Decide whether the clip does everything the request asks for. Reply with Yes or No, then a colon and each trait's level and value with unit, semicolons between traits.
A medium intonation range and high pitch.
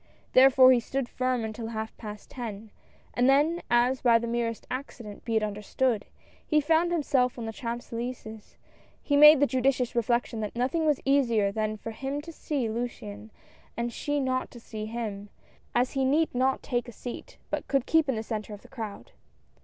Yes: average, 3.4 semitones; high, 240 Hz